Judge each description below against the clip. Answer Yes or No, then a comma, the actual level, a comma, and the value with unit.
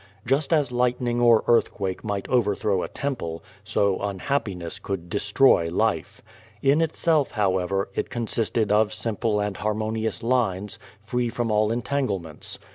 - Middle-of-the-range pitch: No, low, 110 Hz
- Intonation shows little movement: No, average, 3.8 semitones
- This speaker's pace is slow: Yes, slow, 130 wpm